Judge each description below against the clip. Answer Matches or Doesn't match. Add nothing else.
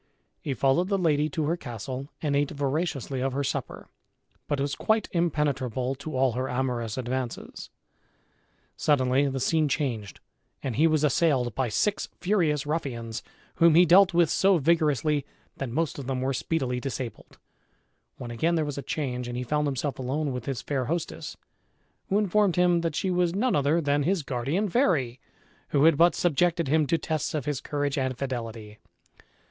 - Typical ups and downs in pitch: Matches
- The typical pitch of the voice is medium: Matches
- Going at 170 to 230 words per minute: Matches